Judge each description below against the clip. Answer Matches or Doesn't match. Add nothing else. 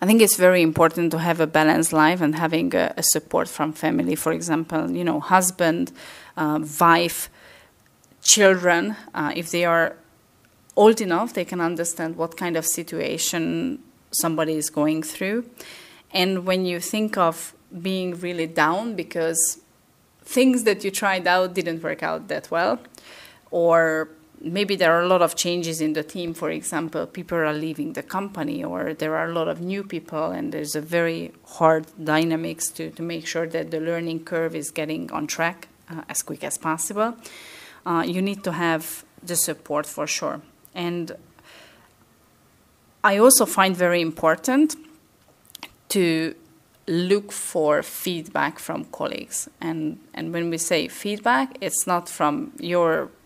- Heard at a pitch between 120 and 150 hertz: Doesn't match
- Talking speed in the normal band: Matches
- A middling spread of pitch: Doesn't match